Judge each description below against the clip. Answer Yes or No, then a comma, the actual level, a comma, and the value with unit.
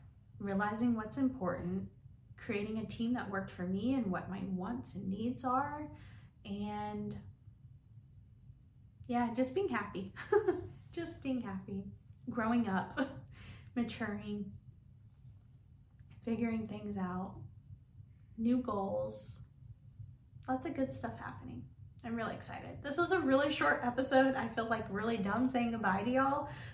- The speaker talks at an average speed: No, slow, 125 wpm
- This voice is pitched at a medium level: No, high, 200 Hz